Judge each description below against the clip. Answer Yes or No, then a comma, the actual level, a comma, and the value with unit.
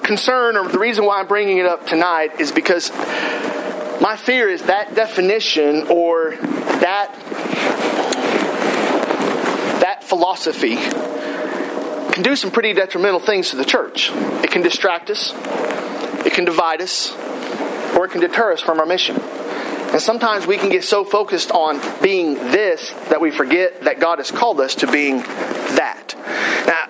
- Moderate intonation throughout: Yes, average, 4.5 semitones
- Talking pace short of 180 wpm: Yes, average, 150 wpm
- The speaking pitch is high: Yes, high, 200 Hz